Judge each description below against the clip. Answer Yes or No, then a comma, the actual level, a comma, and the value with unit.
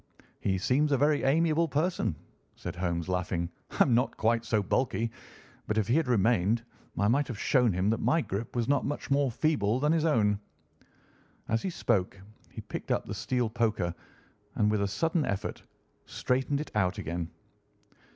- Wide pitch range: Yes, wide, 6.0 semitones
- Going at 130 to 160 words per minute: No, average, 180 wpm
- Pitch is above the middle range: No, low, 115 Hz